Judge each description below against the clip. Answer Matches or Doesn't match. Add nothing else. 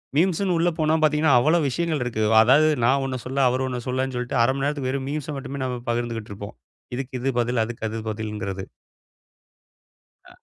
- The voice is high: Doesn't match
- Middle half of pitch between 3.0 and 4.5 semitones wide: Matches